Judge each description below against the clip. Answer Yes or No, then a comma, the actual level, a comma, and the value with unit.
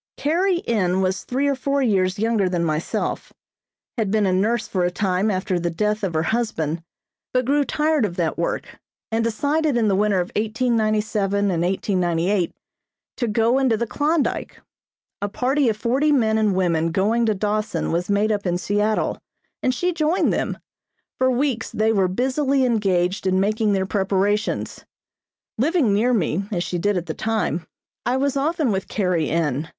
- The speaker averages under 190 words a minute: Yes, average, 175 wpm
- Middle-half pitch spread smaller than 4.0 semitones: No, average, 5.0 semitones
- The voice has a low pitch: No, high, 210 Hz